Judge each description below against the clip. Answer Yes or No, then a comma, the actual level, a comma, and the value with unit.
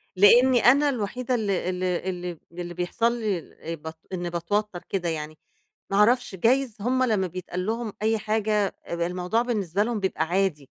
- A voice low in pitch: No, high, 195 Hz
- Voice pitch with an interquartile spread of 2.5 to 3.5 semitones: No, average, 4.4 semitones